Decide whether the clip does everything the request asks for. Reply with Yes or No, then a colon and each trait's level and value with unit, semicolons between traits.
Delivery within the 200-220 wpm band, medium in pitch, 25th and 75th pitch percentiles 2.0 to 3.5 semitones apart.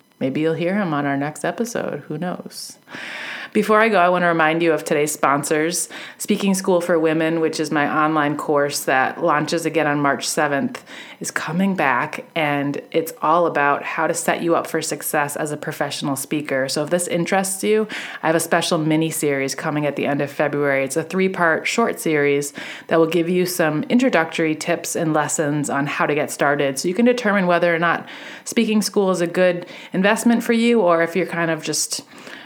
Yes: fast, 205 wpm; medium, 160 Hz; average, 3.2 semitones